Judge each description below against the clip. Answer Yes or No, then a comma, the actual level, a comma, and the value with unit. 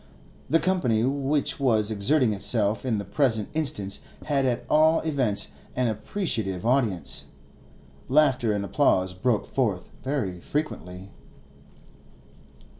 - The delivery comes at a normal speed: No, slow, 115 wpm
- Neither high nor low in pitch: No, low, 120 Hz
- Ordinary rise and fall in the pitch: No, wide, 5.8 semitones